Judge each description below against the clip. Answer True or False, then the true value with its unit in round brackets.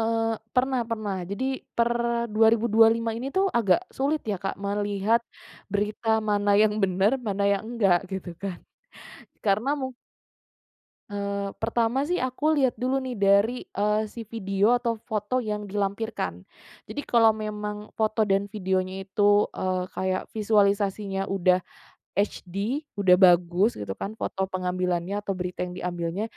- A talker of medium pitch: False (210 Hz)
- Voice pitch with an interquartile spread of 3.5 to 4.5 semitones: False (2.8 semitones)